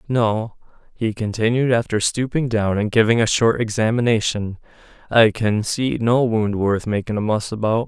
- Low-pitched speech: Yes, low, 110 Hz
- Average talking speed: Yes, average, 160 wpm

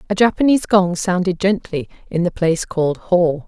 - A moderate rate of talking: Yes, average, 175 wpm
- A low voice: No, medium, 185 Hz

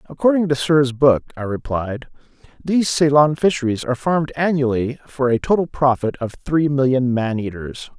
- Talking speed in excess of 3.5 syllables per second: Yes, 5.1 syllables/s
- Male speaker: Yes, male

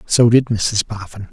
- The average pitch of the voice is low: Yes, low, 110 Hz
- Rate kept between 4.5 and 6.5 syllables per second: No, 4.2 syllables/s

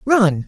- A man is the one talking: Yes, male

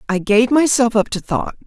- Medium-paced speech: No, fast, 215 wpm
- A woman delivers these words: Yes, female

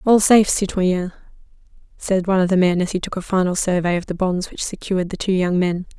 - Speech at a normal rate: No, fast, 230 wpm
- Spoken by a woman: Yes, female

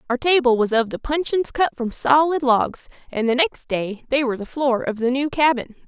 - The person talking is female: Yes, female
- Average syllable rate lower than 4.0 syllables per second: No, 5.1 syllables/s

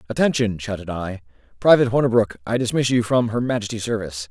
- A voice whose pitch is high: No, low, 110 Hz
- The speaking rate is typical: Yes, average, 165 wpm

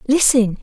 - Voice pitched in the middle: No, high, 245 Hz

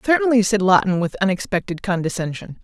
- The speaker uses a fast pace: No, slow, 135 wpm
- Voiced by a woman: Yes, female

